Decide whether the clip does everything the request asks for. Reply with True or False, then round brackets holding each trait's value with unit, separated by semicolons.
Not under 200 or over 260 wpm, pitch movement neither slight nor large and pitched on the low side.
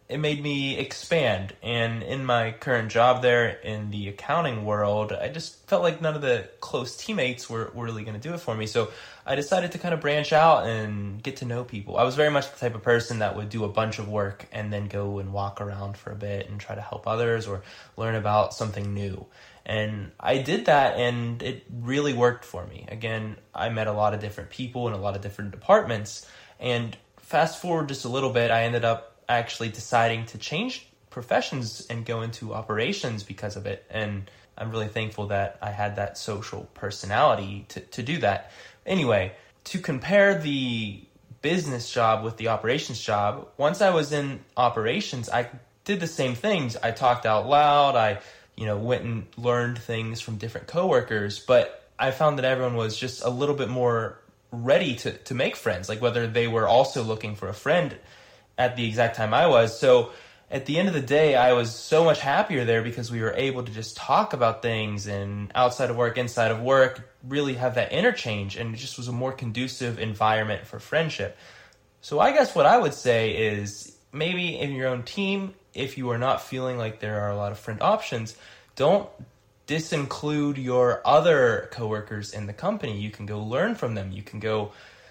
True (205 wpm; 3.9 semitones; 115 Hz)